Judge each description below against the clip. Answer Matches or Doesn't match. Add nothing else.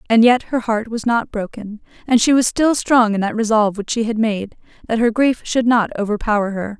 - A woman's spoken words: Matches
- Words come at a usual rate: Doesn't match